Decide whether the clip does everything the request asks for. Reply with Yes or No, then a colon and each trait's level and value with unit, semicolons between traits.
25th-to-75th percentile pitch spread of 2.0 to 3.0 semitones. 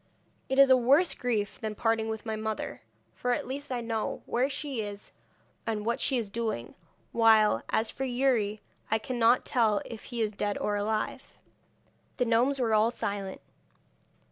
Yes: narrow, 2.6 semitones